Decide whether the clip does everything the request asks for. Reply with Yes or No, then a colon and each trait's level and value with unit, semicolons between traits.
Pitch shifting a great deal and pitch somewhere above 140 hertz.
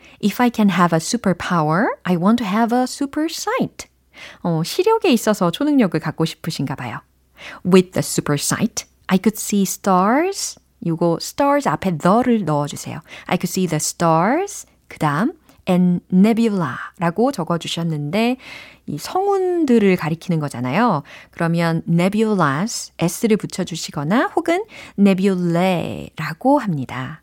Yes: wide, 6.0 semitones; medium, 185 Hz